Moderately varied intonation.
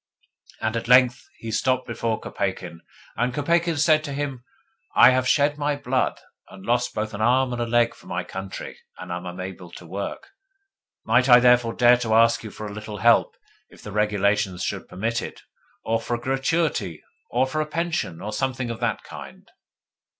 Yes: average, 3.7 semitones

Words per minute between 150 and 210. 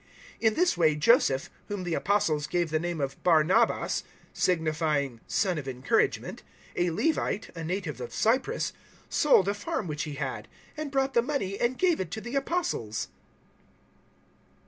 Yes: average, 170 wpm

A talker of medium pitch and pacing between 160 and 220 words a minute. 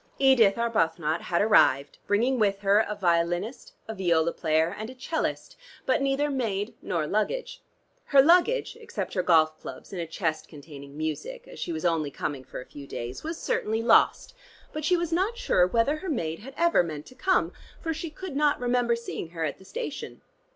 No: high, 210 Hz; average, 195 wpm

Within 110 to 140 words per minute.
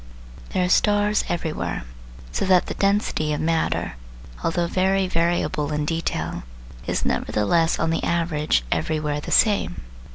Yes: slow, 135 wpm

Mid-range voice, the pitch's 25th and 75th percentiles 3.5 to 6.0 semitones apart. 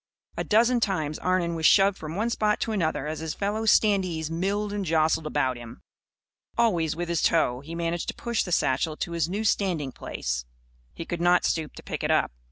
Yes: medium, 170 Hz; average, 4.3 semitones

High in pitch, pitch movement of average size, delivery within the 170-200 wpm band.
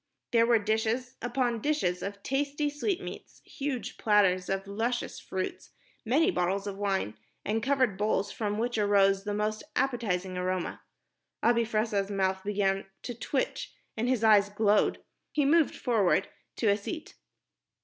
No: high, 215 Hz; average, 3.7 semitones; average, 145 wpm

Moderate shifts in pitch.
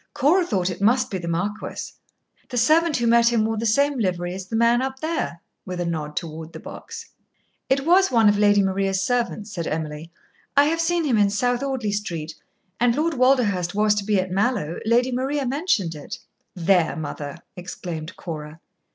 No: wide, 6.3 semitones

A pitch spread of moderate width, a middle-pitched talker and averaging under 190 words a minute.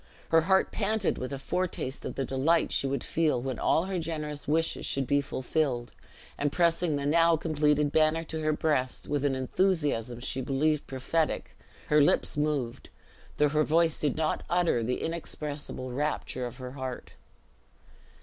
Yes: average, 3.4 semitones; medium, 150 Hz; average, 165 wpm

